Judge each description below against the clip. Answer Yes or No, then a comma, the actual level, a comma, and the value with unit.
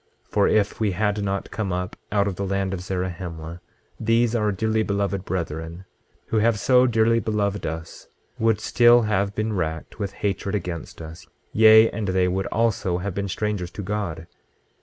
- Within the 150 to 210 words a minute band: Yes, average, 180 wpm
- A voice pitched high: No, low, 100 Hz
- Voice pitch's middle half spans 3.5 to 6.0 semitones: No, average, 3.1 semitones